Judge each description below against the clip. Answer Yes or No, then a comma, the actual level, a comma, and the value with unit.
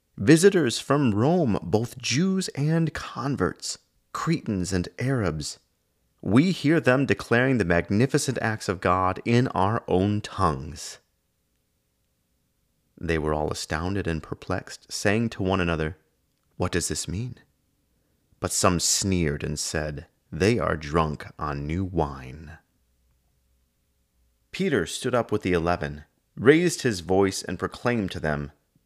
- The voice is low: Yes, very low, 90 Hz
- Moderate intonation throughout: No, wide, 7.7 semitones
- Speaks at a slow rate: Yes, slow, 125 wpm